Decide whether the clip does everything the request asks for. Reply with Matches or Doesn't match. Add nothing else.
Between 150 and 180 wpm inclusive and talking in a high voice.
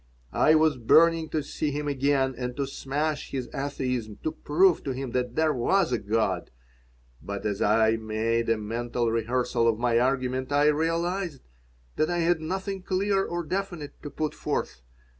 Doesn't match